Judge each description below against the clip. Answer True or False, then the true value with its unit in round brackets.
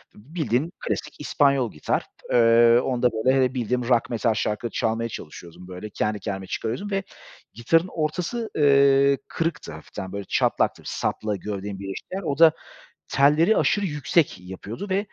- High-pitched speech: False (125 Hz)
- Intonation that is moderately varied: False (6.0 semitones)